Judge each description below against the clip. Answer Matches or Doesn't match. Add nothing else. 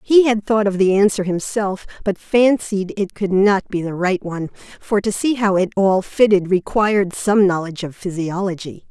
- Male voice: Doesn't match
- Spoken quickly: Doesn't match